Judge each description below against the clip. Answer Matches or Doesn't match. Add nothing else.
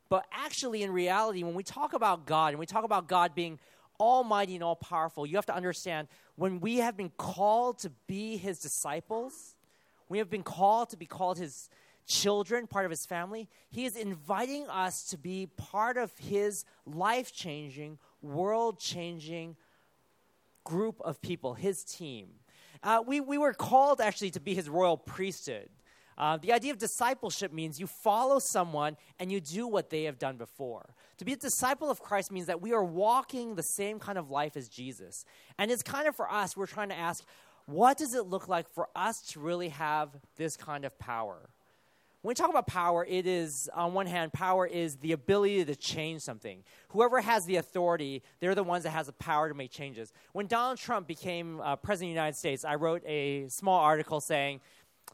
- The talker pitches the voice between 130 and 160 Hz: Doesn't match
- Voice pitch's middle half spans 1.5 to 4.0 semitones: Doesn't match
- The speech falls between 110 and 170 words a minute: Doesn't match